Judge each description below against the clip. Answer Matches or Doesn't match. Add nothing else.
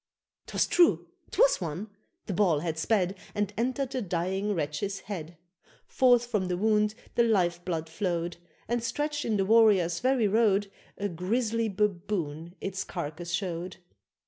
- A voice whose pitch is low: Doesn't match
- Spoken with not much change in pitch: Doesn't match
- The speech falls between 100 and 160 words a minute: Matches